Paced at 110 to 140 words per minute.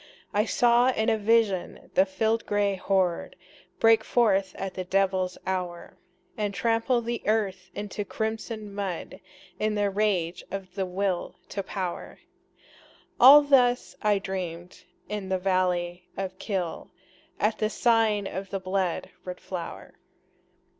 Yes: slow, 135 wpm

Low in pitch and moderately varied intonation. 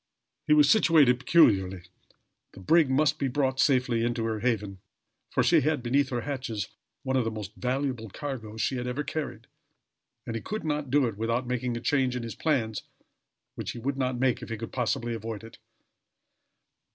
Yes: low, 125 Hz; average, 3.6 semitones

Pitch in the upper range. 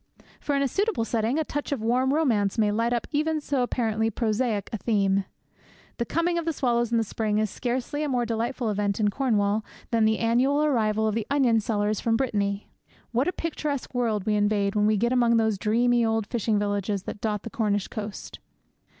Yes: high, 225 Hz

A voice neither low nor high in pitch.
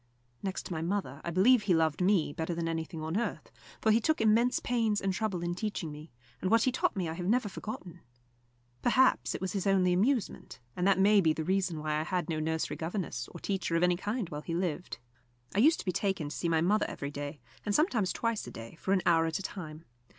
Yes: medium, 180 Hz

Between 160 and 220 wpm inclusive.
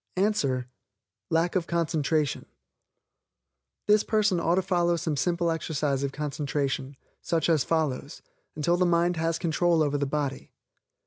No: average, 140 wpm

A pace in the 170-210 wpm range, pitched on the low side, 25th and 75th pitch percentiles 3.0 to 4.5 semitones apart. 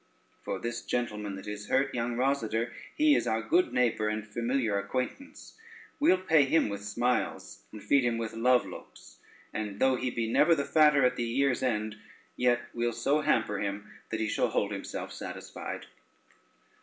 Yes: average, 175 wpm; low, 120 Hz; average, 3.6 semitones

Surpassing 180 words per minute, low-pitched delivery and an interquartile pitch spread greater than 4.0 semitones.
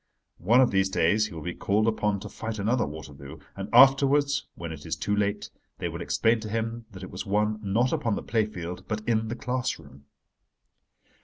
No: average, 200 wpm; low, 105 Hz; average, 3.1 semitones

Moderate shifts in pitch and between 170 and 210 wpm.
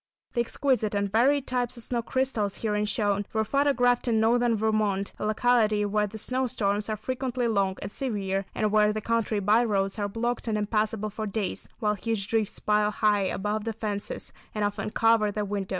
No: narrow, 2.3 semitones; average, 195 wpm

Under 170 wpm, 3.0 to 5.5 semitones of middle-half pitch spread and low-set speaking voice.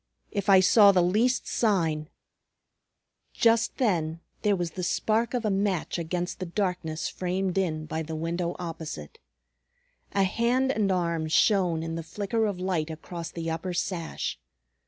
No: average, 155 wpm; average, 3.6 semitones; medium, 180 Hz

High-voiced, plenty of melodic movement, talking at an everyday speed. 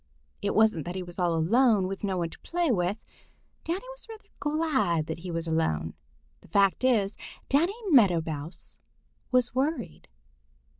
Yes: high, 195 Hz; wide, 7.6 semitones; average, 160 wpm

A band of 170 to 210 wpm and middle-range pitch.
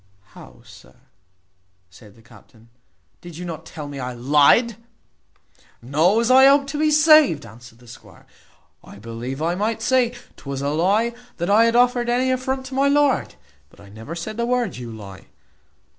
Yes: average, 180 wpm; medium, 175 Hz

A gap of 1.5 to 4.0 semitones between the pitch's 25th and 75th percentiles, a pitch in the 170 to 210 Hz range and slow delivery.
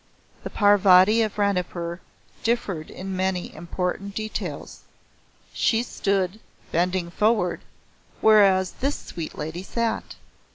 Yes: average, 3.0 semitones; high, 190 Hz; slow, 100 wpm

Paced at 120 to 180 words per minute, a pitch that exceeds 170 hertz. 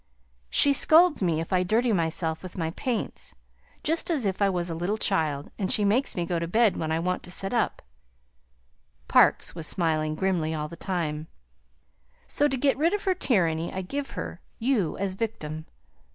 No: average, 190 wpm; medium, 185 Hz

